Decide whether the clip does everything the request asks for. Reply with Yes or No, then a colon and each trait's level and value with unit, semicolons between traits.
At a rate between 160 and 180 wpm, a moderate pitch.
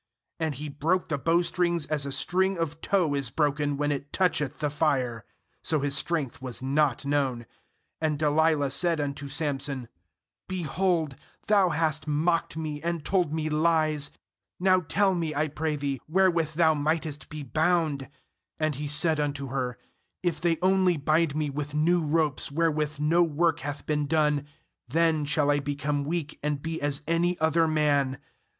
Yes: average, 165 wpm; medium, 150 Hz